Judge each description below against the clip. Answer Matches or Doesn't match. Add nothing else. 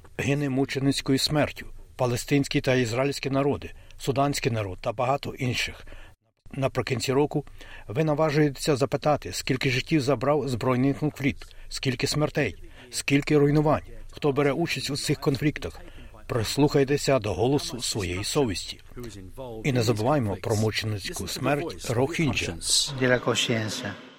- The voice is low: Matches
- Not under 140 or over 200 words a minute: Doesn't match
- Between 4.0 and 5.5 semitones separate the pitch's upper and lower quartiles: Matches